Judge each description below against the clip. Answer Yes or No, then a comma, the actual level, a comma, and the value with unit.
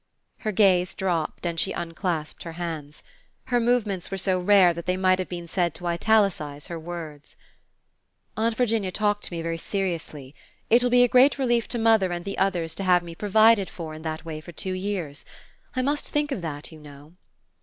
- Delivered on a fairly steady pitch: No, average, 4.2 semitones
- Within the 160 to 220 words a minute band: Yes, average, 200 wpm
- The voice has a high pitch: No, medium, 180 Hz